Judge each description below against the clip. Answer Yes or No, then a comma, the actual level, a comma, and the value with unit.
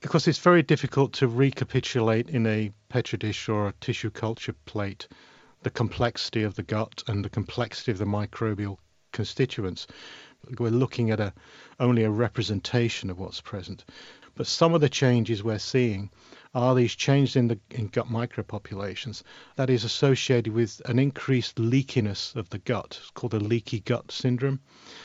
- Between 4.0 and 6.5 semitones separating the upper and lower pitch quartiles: No, average, 3.3 semitones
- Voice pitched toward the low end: Yes, low, 115 Hz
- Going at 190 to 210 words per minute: No, average, 165 wpm